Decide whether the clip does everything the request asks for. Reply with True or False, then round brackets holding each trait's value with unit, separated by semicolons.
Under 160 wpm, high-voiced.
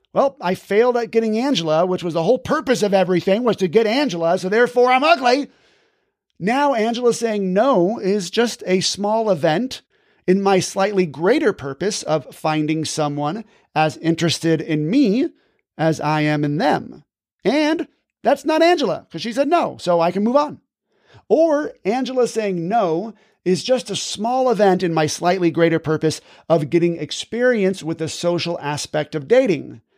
False (165 wpm; 195 Hz)